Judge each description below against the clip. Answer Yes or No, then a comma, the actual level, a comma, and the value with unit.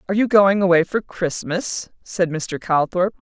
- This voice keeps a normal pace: Yes, average, 165 wpm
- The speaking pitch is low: No, medium, 185 Hz